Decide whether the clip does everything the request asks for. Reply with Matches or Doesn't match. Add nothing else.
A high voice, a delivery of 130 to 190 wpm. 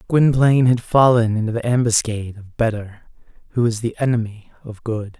Doesn't match